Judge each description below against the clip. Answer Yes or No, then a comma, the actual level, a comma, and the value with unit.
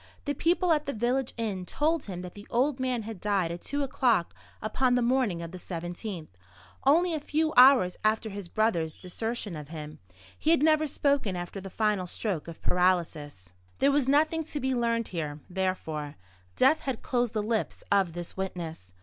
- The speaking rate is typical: Yes, average, 185 wpm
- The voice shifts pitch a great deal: Yes, wide, 7.1 semitones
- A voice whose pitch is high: Yes, high, 215 Hz